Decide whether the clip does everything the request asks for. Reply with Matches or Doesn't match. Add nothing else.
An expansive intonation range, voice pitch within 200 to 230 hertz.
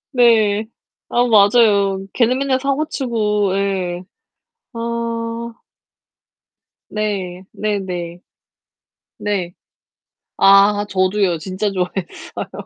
Doesn't match